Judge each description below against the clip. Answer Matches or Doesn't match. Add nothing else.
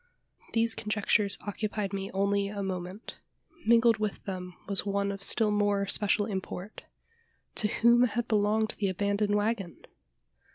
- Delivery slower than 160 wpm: Matches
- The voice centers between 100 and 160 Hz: Doesn't match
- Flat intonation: Matches